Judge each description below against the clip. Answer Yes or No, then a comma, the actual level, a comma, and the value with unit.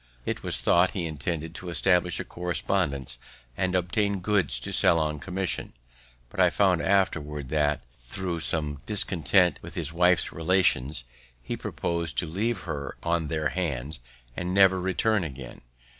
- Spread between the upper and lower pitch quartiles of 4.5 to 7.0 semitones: No, average, 3.6 semitones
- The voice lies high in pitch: No, very low, 85 Hz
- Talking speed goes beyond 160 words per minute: No, average, 150 wpm